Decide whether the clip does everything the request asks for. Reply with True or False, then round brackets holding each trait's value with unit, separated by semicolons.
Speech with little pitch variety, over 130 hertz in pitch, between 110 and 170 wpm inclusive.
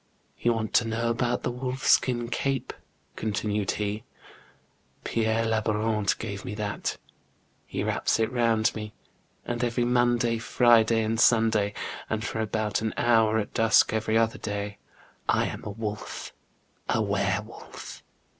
False (1.6 semitones; 110 Hz; 155 wpm)